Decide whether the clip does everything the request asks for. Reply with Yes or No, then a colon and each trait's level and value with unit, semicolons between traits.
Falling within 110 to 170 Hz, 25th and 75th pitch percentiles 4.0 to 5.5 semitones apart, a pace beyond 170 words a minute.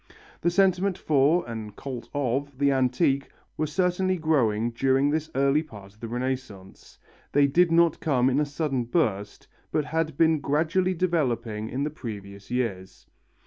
No: medium, 140 Hz; average, 5.2 semitones; average, 155 wpm